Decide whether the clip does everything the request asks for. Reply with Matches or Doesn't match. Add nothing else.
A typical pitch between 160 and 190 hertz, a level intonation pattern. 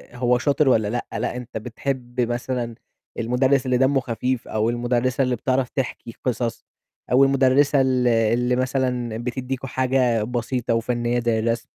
Doesn't match